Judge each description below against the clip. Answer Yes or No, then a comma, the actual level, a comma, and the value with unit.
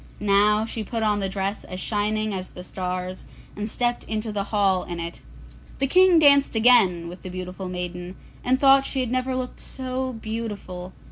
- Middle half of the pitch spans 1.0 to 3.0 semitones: No, average, 5.1 semitones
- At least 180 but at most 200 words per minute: Yes, average, 185 wpm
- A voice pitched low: No, high, 210 Hz